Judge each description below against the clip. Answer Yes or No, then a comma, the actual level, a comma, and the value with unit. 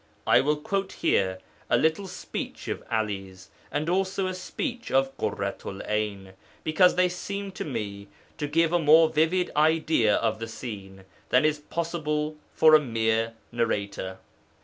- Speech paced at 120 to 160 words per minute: Yes, average, 150 wpm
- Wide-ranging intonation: Yes, wide, 7.6 semitones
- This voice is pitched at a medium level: Yes, medium, 150 Hz